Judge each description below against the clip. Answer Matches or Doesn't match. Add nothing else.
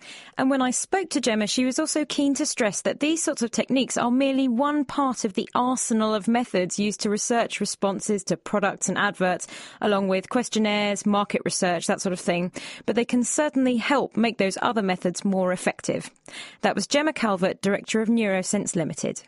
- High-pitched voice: Matches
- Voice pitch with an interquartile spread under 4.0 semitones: Doesn't match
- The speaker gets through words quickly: Doesn't match